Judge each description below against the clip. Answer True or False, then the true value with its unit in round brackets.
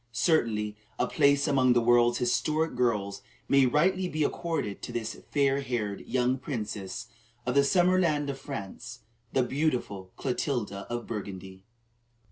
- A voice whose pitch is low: True (125 Hz)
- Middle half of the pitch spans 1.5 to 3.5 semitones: False (4.4 semitones)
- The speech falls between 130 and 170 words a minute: True (140 wpm)